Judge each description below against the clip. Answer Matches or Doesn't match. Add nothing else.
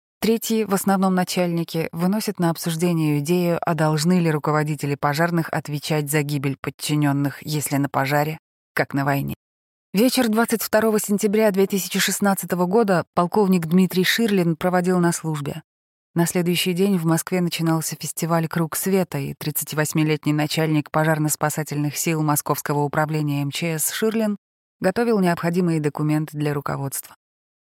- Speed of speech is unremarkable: Matches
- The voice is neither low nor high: Matches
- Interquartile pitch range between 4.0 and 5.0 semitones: Doesn't match